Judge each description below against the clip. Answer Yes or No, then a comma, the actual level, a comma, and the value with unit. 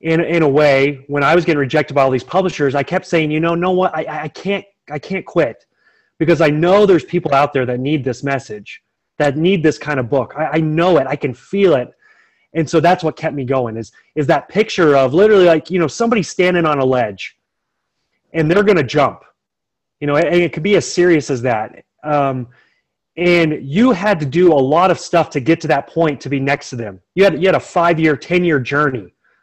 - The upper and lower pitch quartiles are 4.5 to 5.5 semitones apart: No, average, 4.0 semitones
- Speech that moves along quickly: Yes, fast, 235 wpm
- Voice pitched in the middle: Yes, medium, 155 Hz